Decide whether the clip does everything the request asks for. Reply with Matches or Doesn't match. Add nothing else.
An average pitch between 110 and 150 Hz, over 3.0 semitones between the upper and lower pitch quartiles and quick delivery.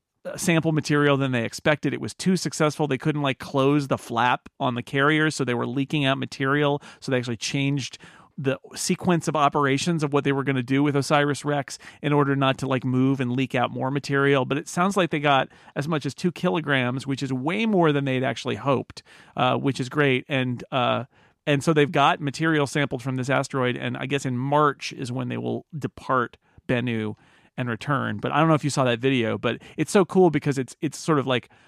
Doesn't match